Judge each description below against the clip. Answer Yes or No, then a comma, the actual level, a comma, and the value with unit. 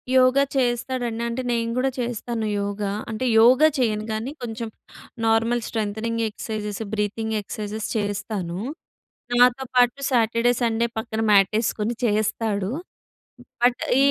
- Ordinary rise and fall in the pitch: No, narrow, 2.2 semitones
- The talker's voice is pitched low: No, high, 225 Hz